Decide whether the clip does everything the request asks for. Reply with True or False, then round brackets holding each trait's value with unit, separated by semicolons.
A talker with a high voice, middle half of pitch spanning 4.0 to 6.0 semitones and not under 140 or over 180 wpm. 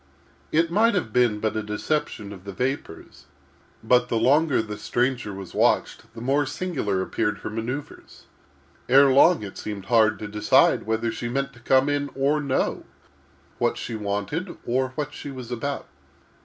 False (125 Hz; 4.9 semitones; 170 wpm)